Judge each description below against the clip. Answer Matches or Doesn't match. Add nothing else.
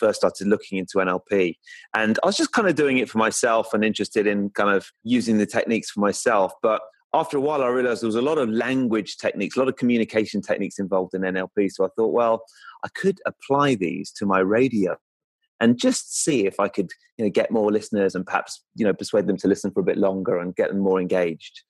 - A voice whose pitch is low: Matches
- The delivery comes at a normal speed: Doesn't match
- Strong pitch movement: Matches